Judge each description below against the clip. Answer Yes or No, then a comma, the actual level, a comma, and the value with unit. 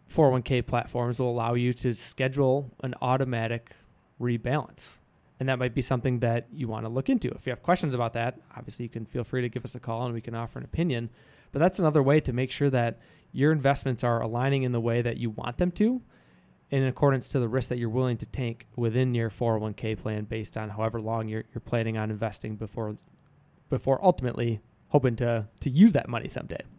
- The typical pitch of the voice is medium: No, low, 125 Hz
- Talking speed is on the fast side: Yes, fast, 215 wpm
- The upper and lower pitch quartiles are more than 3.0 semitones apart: No, average, 2.7 semitones